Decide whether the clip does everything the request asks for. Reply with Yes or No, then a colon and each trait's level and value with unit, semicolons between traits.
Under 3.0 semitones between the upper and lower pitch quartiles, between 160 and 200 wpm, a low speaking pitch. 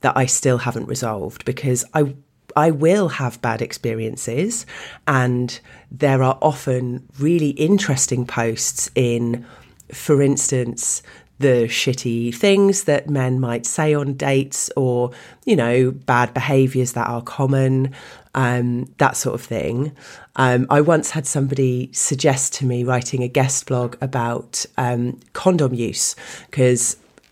No: narrow, 2.4 semitones; slow, 135 wpm; low, 130 Hz